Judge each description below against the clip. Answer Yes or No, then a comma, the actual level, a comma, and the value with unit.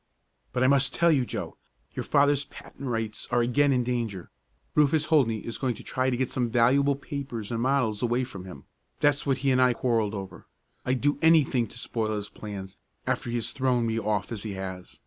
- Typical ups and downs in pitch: Yes, average, 3.8 semitones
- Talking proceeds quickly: Yes, fast, 210 wpm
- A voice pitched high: No, low, 125 Hz